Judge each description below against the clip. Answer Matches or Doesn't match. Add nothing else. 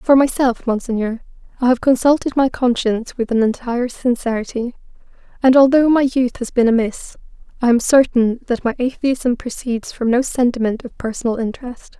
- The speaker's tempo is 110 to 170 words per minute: Matches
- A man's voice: Doesn't match